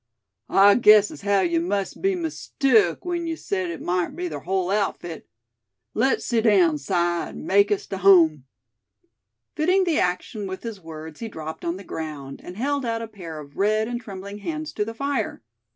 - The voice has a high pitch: Yes, high, 200 Hz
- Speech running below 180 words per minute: No, average, 195 wpm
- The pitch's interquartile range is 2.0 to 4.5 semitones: No, average, 4.9 semitones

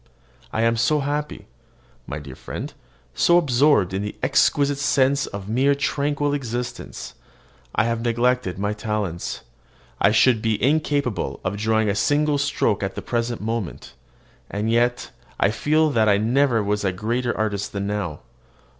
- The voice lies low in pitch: Yes, low, 115 Hz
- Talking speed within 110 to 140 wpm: No, average, 155 wpm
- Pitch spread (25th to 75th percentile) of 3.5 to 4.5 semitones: No, average, 5.2 semitones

